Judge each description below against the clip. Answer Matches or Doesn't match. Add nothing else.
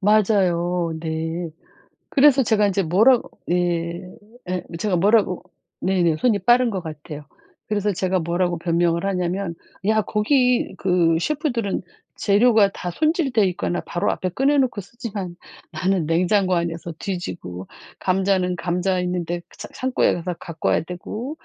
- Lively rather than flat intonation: Doesn't match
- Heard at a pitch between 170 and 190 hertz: Matches